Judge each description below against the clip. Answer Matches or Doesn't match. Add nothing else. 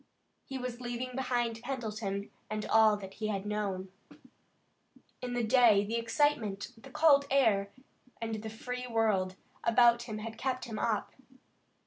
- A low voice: Doesn't match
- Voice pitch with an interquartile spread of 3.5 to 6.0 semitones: Doesn't match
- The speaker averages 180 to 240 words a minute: Doesn't match